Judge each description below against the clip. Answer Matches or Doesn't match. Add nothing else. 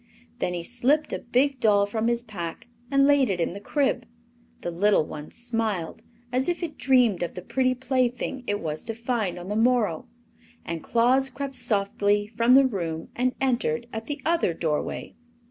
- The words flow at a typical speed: Matches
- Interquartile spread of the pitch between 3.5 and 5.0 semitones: Matches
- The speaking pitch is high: Matches